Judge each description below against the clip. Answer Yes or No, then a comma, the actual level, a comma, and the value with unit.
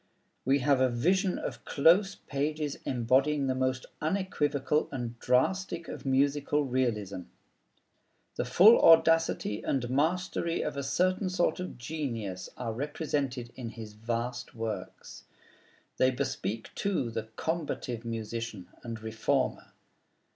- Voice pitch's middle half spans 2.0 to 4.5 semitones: No, average, 5.3 semitones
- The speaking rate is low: Yes, slow, 120 wpm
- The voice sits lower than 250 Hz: Yes, low, 135 Hz